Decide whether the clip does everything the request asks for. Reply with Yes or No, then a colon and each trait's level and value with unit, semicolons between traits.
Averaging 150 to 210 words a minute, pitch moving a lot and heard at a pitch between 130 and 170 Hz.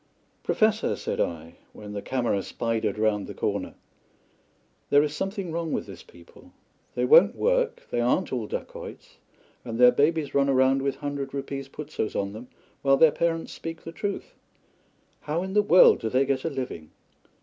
Yes: average, 170 wpm; wide, 6.7 semitones; medium, 140 Hz